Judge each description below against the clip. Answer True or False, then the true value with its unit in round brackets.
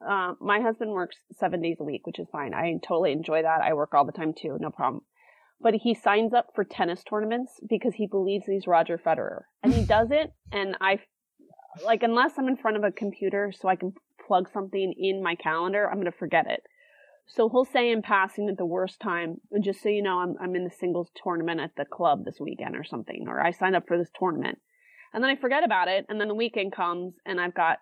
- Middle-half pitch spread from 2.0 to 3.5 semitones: False (4.2 semitones)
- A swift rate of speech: True (240 wpm)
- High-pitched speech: True (195 Hz)